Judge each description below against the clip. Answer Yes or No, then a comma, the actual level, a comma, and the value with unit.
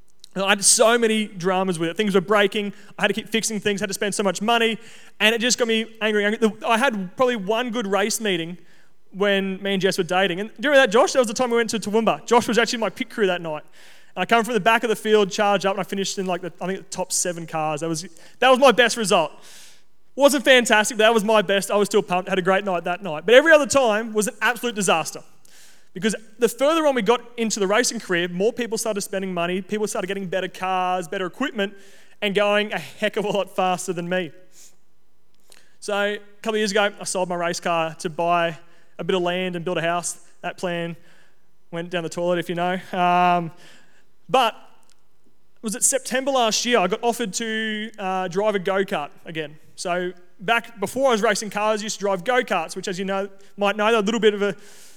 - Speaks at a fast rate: Yes, fast, 245 wpm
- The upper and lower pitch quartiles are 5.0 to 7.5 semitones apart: No, average, 3.4 semitones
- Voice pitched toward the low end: No, high, 200 Hz